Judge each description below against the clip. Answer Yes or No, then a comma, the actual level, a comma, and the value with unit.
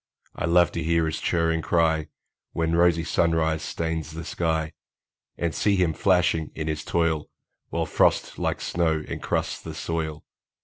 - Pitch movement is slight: Yes, narrow, 1.0 semitones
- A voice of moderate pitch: No, very low, 80 Hz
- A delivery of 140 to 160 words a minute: Yes, average, 150 wpm